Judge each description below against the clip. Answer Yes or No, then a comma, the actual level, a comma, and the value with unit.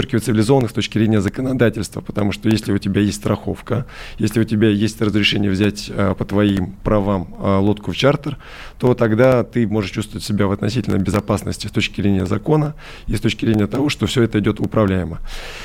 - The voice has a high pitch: No, low, 105 Hz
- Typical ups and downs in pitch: No, narrow, 2.1 semitones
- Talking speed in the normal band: No, fast, 180 wpm